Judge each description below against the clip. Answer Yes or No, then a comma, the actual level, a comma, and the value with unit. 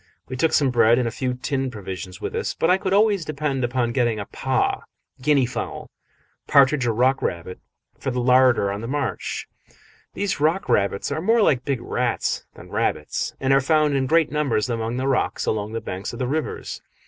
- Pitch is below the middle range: Yes, low, 130 Hz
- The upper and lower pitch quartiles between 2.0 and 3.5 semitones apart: No, average, 4.2 semitones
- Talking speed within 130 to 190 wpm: No, average, 200 wpm